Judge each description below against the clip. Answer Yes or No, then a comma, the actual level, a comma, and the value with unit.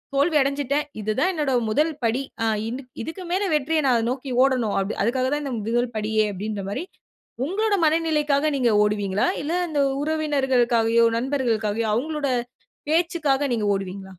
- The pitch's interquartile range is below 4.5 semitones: No, average, 5.0 semitones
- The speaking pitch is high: Yes, very high, 265 Hz